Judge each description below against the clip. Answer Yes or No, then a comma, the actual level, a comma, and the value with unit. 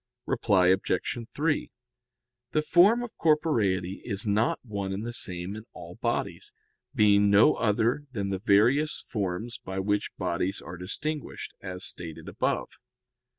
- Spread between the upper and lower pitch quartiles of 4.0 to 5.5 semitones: Yes, average, 4.7 semitones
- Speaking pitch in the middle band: No, low, 105 Hz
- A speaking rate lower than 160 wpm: Yes, average, 140 wpm